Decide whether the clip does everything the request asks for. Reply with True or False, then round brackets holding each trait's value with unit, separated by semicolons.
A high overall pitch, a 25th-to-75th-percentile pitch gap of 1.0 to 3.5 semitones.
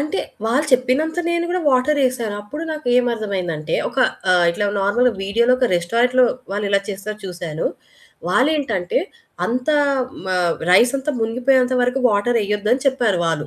False (240 Hz; 4.4 semitones)